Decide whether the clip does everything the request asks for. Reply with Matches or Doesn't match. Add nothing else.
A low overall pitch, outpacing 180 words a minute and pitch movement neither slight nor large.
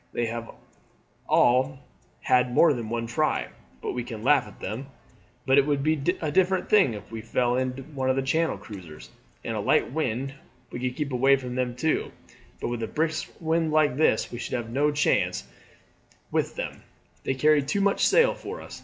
Matches